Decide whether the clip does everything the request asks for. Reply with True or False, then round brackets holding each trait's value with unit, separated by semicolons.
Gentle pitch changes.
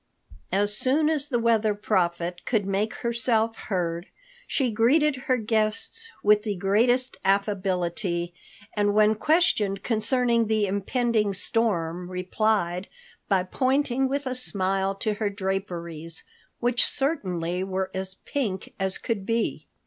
False (3.9 semitones)